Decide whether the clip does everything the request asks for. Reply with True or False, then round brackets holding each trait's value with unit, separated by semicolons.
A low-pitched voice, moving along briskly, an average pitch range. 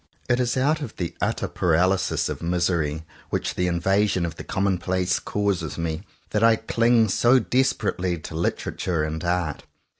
False (90 Hz; 155 wpm; 4.2 semitones)